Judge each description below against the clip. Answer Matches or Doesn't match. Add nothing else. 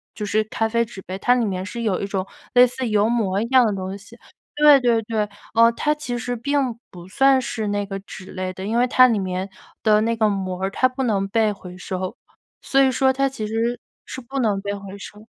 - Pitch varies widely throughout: Doesn't match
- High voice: Matches